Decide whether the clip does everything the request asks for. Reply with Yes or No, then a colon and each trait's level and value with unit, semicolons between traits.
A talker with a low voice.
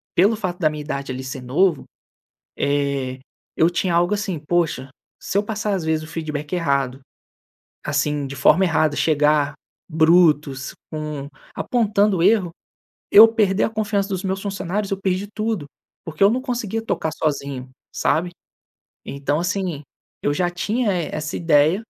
No: medium, 165 Hz